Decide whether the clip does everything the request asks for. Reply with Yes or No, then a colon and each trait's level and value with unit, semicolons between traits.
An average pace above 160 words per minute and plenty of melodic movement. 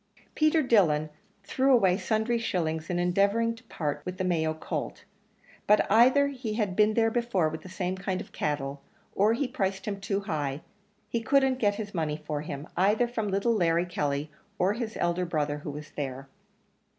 Yes: average, 185 wpm; wide, 6.2 semitones